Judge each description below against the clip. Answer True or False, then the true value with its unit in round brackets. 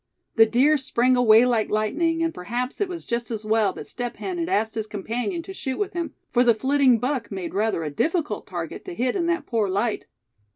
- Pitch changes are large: True (6.9 semitones)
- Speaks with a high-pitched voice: True (245 Hz)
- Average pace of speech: False (220 wpm)